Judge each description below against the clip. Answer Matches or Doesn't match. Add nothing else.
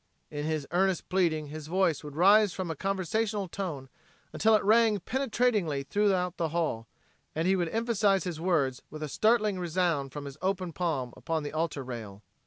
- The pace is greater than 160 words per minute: Matches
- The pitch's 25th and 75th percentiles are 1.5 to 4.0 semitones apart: Doesn't match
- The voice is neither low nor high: Matches